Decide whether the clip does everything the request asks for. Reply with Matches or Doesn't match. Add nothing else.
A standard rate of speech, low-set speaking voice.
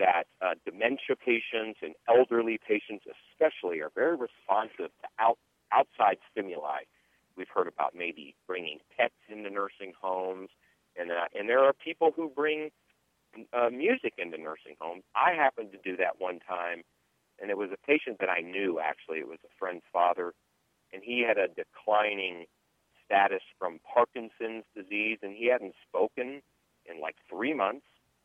Matches